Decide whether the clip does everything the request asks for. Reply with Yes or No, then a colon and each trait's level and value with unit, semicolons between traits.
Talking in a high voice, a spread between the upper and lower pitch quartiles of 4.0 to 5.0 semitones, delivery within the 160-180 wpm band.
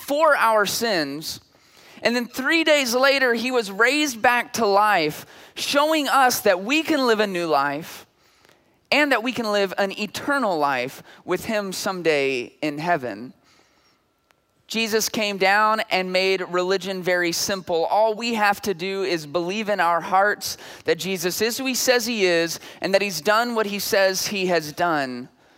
Yes: high, 200 Hz; average, 4.7 semitones; average, 170 wpm